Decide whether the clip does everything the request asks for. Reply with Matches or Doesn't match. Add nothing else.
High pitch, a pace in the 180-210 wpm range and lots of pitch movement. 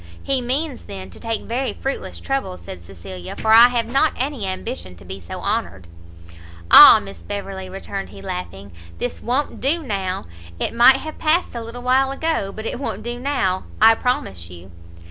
Matches